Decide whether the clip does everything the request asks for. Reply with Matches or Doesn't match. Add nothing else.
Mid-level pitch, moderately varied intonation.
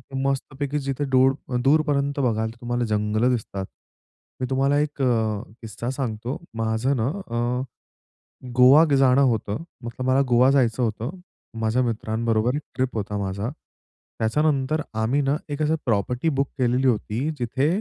Doesn't match